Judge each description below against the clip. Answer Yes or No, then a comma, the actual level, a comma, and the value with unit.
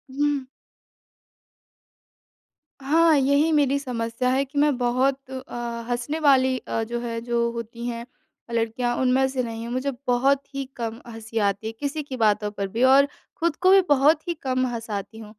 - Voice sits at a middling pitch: No, very high, 250 Hz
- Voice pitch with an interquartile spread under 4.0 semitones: Yes, average, 3.1 semitones